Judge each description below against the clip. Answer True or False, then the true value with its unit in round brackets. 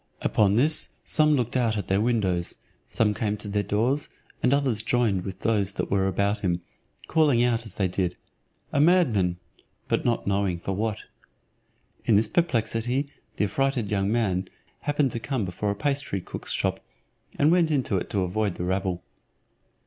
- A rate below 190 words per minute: True (170 wpm)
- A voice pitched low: True (110 Hz)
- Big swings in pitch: False (4.6 semitones)